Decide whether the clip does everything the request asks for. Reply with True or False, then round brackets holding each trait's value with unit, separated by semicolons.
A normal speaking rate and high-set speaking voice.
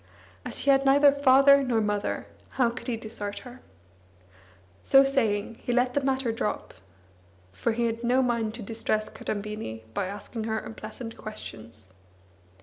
True (150 wpm; 230 Hz)